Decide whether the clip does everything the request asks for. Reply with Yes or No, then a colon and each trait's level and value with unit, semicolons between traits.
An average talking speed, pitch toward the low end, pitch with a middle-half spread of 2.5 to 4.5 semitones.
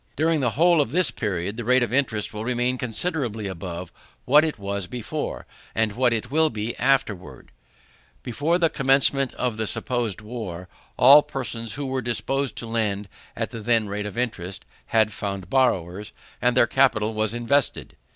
Yes: average, 170 wpm; low, 120 Hz; average, 4.2 semitones